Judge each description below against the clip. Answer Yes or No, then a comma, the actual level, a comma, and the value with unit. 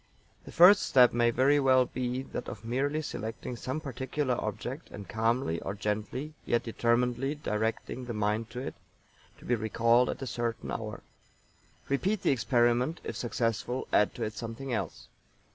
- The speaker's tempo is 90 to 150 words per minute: No, average, 160 wpm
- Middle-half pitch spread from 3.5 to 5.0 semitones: No, average, 2.7 semitones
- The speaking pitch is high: No, low, 120 Hz